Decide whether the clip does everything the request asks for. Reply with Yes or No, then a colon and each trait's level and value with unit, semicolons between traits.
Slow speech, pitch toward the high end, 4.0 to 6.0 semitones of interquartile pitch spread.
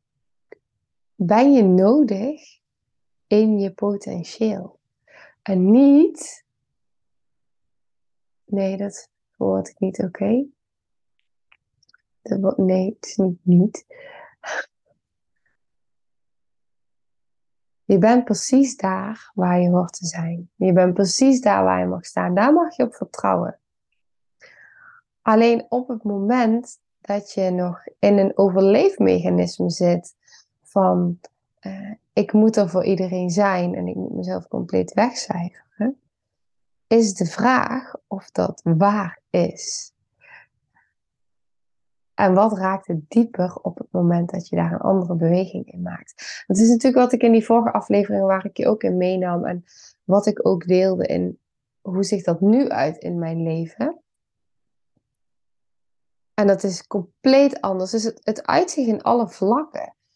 Yes: slow, 130 wpm; high, 195 Hz; average, 4.4 semitones